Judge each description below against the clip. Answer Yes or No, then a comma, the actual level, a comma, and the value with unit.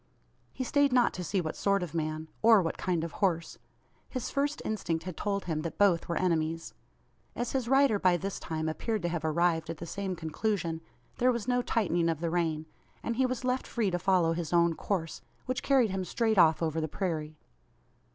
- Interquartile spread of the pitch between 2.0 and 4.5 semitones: No, average, 5.3 semitones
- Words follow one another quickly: Yes, fast, 210 wpm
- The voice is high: No, medium, 180 Hz